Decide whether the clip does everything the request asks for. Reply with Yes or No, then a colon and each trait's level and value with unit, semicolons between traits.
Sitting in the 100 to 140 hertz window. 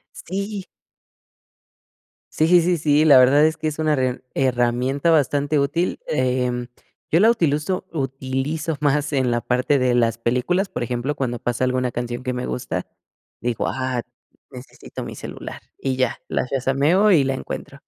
Yes: low, 135 Hz